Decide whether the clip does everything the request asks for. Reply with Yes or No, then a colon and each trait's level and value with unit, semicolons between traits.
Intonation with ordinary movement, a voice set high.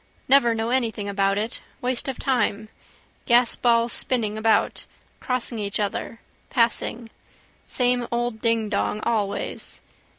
No: narrow, 2.2 semitones; high, 230 Hz